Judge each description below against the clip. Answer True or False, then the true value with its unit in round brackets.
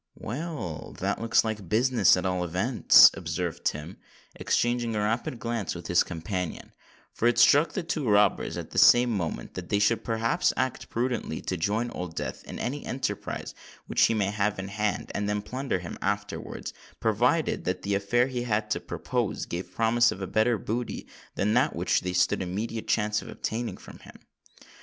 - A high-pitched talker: False (105 Hz)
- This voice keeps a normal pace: True (180 wpm)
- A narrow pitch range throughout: False (3.8 semitones)